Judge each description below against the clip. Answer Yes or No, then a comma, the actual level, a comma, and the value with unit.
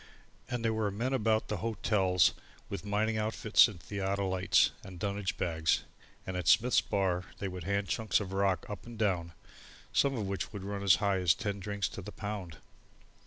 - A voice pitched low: Yes, low, 100 Hz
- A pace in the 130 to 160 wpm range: No, average, 185 wpm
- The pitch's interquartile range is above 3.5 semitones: No, narrow, 2.5 semitones